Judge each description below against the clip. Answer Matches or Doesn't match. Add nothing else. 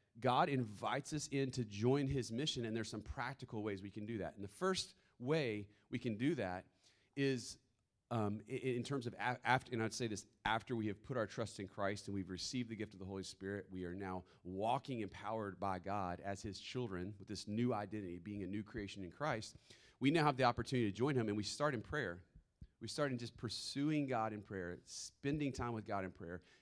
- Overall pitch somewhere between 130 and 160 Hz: Doesn't match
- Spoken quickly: Matches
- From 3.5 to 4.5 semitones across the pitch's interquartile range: Matches